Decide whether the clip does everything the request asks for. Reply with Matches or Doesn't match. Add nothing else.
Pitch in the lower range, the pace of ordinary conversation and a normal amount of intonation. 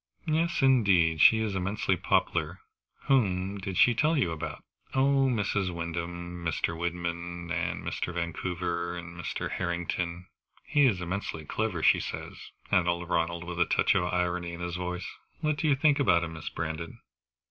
Matches